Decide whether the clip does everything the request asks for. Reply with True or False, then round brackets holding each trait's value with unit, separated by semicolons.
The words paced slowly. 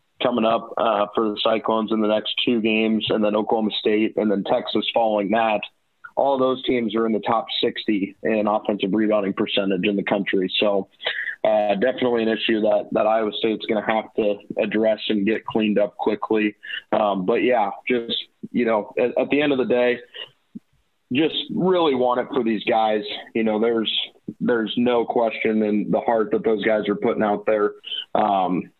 False (190 wpm)